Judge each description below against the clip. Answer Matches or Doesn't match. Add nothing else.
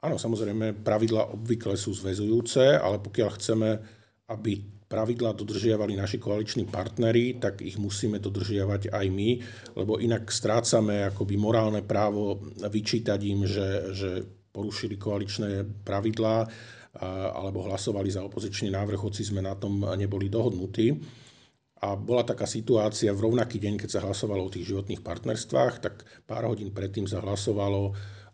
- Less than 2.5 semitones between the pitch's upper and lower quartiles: Matches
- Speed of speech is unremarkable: Matches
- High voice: Doesn't match